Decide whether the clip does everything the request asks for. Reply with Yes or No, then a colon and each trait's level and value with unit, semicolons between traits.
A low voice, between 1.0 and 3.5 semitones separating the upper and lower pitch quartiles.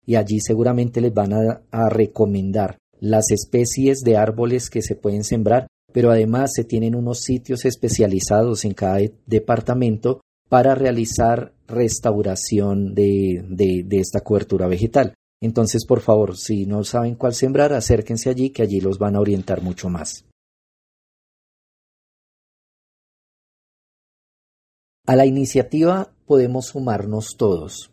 Yes: low, 115 Hz; average, 2.9 semitones